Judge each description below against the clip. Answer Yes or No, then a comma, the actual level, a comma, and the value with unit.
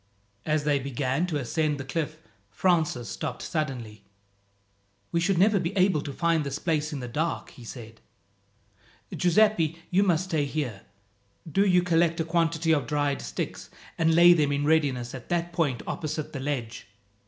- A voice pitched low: No, medium, 155 Hz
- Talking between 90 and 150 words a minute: No, average, 165 wpm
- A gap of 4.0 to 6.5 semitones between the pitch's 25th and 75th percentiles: No, average, 3.5 semitones